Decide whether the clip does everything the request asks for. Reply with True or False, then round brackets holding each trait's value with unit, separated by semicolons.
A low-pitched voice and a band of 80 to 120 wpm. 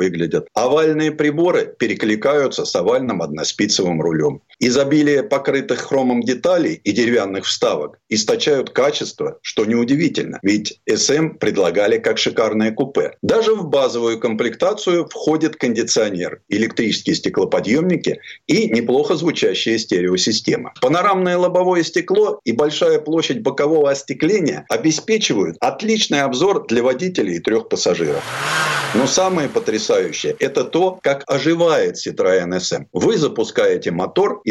False (180 Hz; 115 wpm)